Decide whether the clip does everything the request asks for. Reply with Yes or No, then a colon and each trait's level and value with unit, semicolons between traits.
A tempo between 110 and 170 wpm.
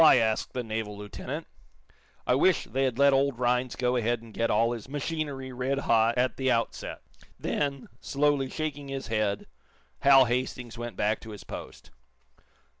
Yes: average, 165 wpm